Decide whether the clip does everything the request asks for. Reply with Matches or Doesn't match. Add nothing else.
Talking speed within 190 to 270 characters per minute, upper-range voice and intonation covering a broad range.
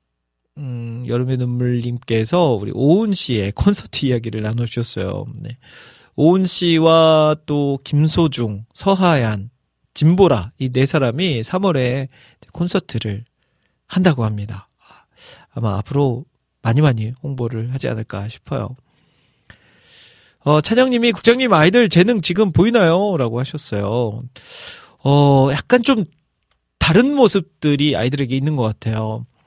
Doesn't match